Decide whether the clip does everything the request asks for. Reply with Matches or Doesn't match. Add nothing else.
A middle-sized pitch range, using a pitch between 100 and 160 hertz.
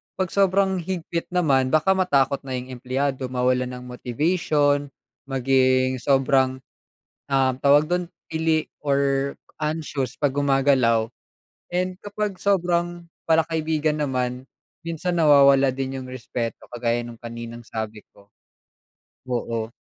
Matches